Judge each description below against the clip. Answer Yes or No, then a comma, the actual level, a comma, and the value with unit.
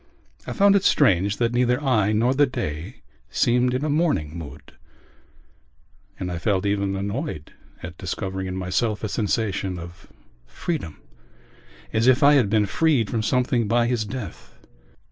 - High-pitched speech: No, low, 110 Hz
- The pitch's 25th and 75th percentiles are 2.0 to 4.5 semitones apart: No, average, 5.0 semitones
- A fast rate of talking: No, average, 155 wpm